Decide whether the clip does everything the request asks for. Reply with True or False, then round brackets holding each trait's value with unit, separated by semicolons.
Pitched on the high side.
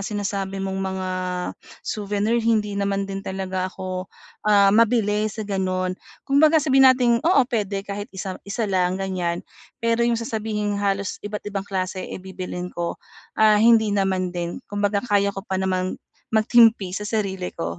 True (200 Hz)